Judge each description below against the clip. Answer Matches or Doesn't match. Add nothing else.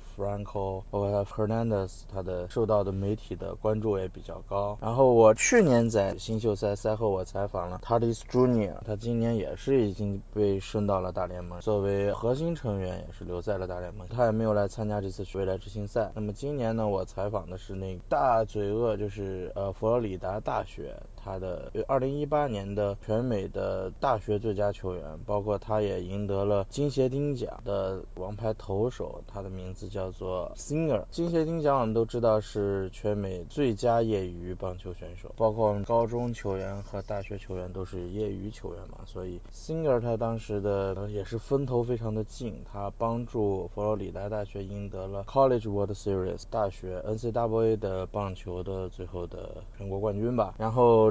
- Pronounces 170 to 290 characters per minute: Doesn't match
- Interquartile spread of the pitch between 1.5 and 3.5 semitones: Matches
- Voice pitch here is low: Matches